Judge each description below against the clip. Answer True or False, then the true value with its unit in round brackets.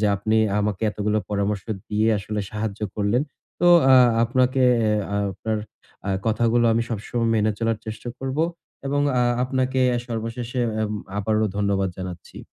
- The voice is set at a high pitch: False (110 Hz)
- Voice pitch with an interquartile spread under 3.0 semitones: True (2.5 semitones)